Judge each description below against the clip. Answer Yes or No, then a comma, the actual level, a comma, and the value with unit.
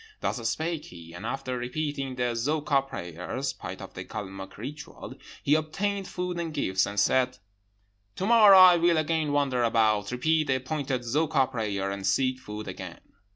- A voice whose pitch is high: No, low, 135 Hz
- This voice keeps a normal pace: Yes, average, 165 wpm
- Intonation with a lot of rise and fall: Yes, wide, 5.8 semitones